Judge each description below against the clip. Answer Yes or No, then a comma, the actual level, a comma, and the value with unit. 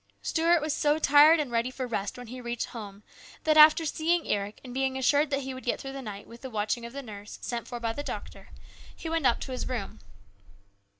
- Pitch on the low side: No, very high, 255 Hz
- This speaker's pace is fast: Yes, fast, 235 wpm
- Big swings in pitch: No, average, 4.1 semitones